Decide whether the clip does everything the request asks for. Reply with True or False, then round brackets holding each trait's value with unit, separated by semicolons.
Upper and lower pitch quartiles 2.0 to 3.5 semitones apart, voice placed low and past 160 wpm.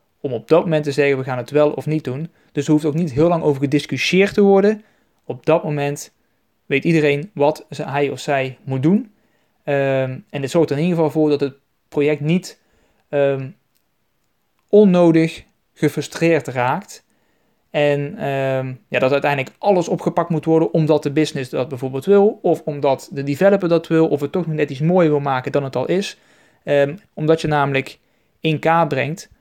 False (2.9 semitones; 150 Hz; 190 wpm)